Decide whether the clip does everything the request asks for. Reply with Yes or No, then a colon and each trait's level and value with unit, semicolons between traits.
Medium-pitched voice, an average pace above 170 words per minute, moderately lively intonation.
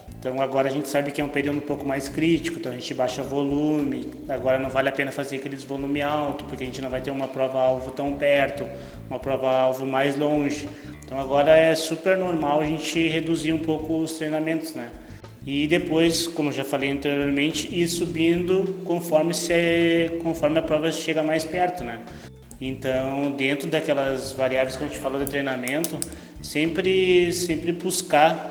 Yes: medium, 145 Hz; fast, 185 wpm; average, 3.1 semitones